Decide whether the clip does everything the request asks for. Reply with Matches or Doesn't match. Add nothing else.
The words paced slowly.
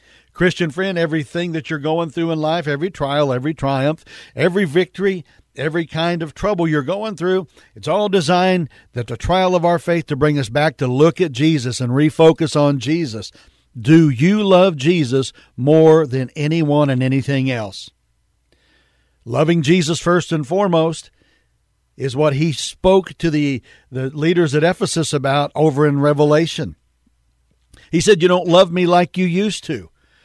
Doesn't match